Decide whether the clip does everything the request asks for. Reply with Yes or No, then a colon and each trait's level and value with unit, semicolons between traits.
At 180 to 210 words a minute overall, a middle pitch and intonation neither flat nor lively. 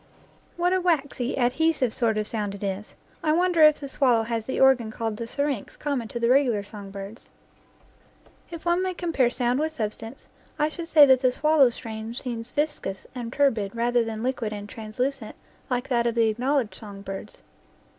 No: average, 190 wpm; high, 245 Hz; average, 4.6 semitones